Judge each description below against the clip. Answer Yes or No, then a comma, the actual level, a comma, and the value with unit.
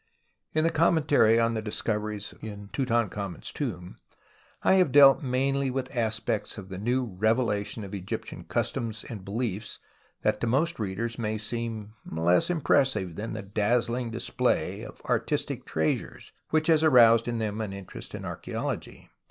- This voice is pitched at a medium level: No, low, 115 Hz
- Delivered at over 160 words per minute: No, average, 150 wpm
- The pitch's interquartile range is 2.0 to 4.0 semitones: Yes, average, 3.7 semitones